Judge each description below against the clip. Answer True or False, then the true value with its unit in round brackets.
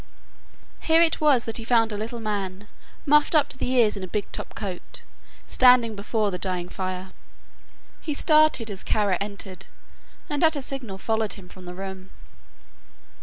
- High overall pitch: True (215 Hz)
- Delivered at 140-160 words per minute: False (170 wpm)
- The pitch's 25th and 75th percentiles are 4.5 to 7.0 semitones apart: True (4.8 semitones)